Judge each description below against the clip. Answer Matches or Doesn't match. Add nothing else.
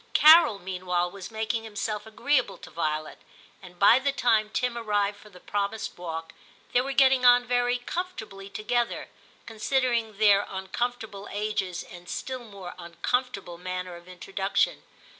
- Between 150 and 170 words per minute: Matches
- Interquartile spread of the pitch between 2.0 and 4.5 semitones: Doesn't match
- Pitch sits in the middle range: Doesn't match